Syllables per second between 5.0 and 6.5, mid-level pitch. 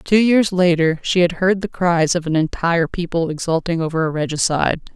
Yes: 5.5 syllables/s; medium, 170 Hz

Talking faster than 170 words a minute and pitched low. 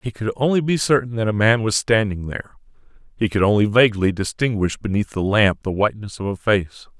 Yes: fast, 205 wpm; low, 110 Hz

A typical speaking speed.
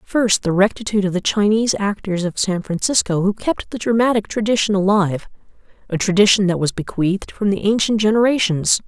Yes: average, 170 wpm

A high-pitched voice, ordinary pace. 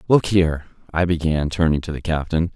No: very low, 80 Hz; average, 190 wpm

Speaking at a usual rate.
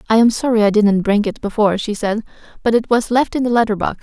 No: fast, 270 wpm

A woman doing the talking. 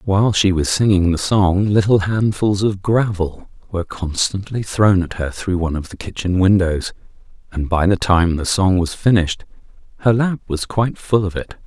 No: male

